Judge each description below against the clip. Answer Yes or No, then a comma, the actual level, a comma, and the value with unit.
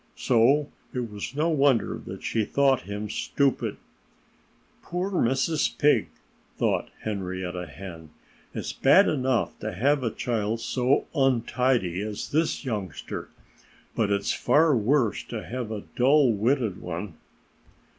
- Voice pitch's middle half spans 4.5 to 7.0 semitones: Yes, average, 5.2 semitones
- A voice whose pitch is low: Yes, low, 120 Hz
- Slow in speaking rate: Yes, slow, 125 wpm